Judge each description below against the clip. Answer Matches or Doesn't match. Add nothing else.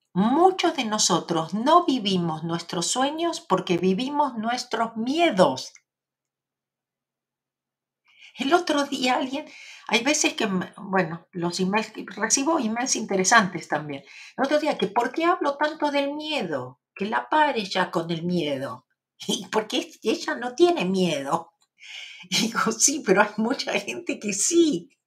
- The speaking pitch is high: Matches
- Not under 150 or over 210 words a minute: Doesn't match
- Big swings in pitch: Matches